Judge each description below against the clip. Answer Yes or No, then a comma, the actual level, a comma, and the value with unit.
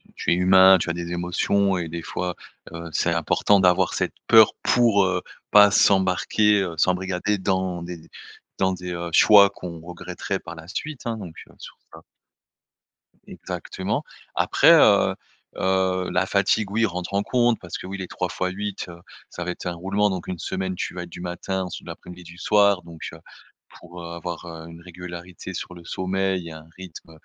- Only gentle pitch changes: Yes, narrow, 1.9 semitones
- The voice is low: Yes, very low, 90 Hz